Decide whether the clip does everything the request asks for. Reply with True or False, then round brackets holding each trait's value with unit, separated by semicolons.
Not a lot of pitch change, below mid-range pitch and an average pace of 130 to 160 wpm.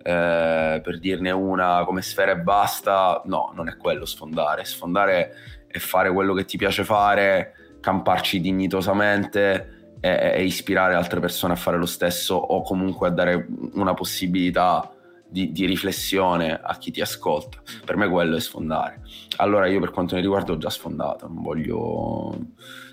True (1.5 semitones; 95 Hz; 155 wpm)